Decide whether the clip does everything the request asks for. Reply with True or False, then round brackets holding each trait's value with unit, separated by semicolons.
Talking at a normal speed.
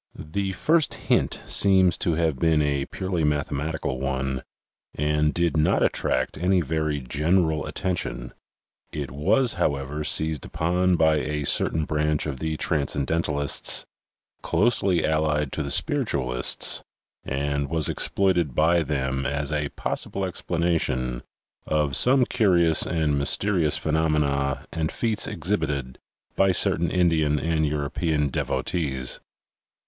False (125 wpm)